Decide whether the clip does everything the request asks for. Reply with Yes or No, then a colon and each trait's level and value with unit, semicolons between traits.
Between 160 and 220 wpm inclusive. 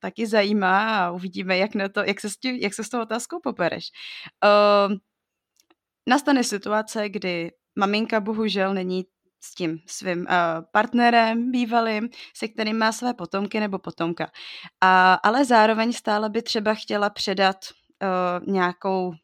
No: average, 145 wpm